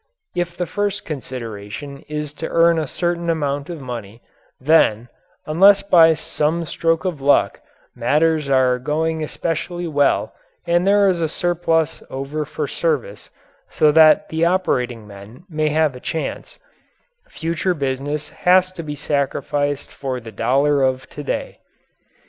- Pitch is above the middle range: No, medium, 150 Hz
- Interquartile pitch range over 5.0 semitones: No, average, 3.7 semitones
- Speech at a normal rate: Yes, average, 145 wpm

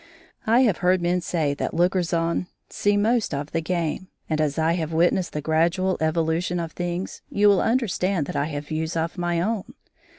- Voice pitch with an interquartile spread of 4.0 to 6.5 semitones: No, average, 2.7 semitones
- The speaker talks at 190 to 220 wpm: Yes, average, 195 wpm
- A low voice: No, medium, 175 Hz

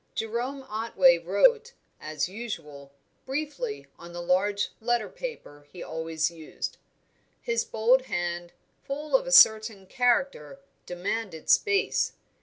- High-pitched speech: Yes, high, 220 Hz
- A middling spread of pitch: No, wide, 8.1 semitones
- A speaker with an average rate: No, slow, 115 wpm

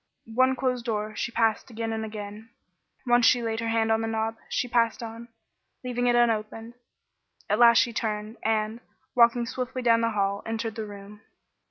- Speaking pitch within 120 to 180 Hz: No, high, 225 Hz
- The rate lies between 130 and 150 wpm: No, average, 190 wpm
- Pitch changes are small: Yes, narrow, 1.6 semitones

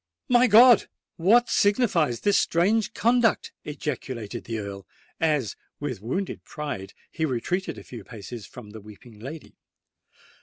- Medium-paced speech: No, slow, 130 wpm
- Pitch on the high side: No, medium, 150 Hz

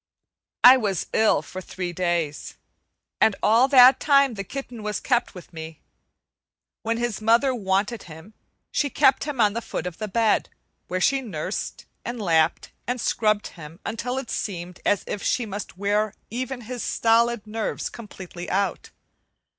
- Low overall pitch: No, high, 215 Hz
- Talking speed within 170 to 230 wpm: No, average, 160 wpm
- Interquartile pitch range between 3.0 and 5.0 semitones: Yes, average, 4.5 semitones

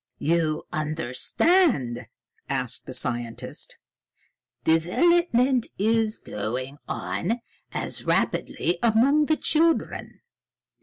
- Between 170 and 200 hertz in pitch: Yes, high, 190 Hz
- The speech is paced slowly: Yes, slow, 80 wpm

